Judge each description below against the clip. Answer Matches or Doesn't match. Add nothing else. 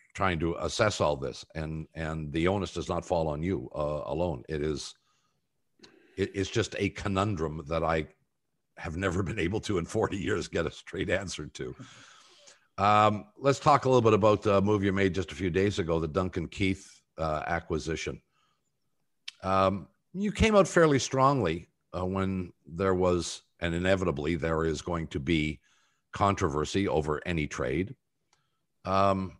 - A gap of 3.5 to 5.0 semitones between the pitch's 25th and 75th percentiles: Matches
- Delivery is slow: Doesn't match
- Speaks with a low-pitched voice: Matches